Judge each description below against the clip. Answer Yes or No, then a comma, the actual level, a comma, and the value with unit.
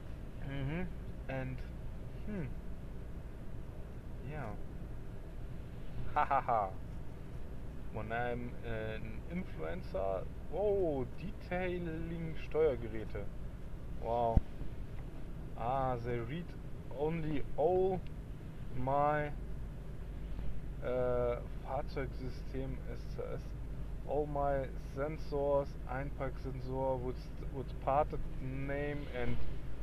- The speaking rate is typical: No, slow, 65 wpm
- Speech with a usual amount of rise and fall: Yes, average, 3.2 semitones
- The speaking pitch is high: No, low, 135 Hz